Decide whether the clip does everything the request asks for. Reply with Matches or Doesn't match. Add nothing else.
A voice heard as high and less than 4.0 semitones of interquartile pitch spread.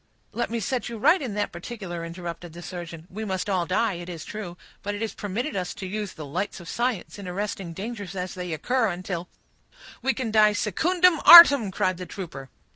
Doesn't match